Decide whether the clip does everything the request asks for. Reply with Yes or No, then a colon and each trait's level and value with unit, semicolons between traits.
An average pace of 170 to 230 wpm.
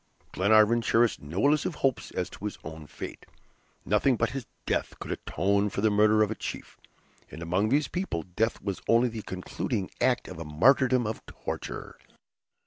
Yes: average, 175 wpm